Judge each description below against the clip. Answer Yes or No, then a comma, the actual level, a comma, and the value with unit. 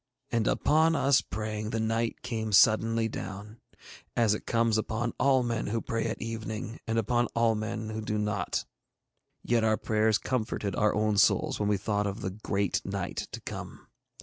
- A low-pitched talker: Yes, low, 110 Hz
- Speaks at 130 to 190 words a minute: Yes, average, 175 wpm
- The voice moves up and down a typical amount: No, narrow, 1.5 semitones